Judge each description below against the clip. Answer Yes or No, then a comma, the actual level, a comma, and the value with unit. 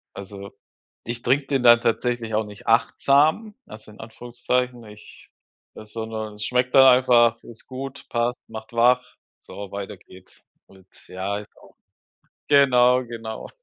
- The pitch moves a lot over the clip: No, average, 2.7 semitones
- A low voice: Yes, low, 120 Hz